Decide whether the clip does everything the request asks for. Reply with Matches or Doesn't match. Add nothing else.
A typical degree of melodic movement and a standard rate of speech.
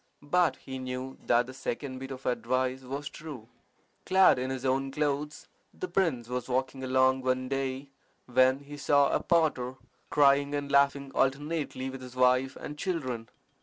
Doesn't match